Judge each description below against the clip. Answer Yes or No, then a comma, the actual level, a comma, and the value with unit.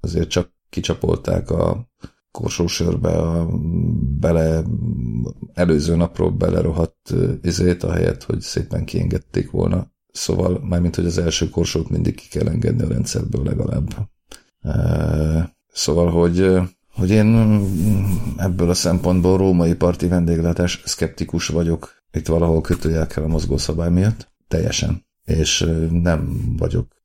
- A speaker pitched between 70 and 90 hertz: Yes, very low, 85 Hz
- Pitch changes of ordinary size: No, narrow, 2.1 semitones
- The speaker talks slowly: No, average, 120 wpm